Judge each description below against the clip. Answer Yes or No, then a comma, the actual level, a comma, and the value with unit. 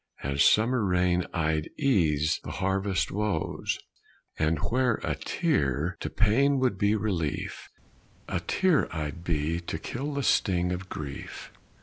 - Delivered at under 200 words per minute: Yes, slow, 135 wpm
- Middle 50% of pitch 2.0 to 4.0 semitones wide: No, wide, 5.6 semitones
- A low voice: Yes, very low, 90 Hz